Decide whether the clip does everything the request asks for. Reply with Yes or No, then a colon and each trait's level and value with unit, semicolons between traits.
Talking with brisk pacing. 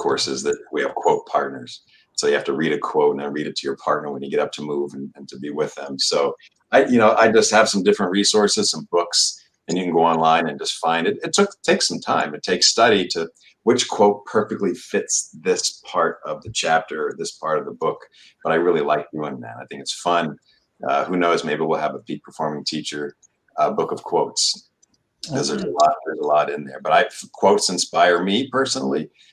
Yes: fast, 235 wpm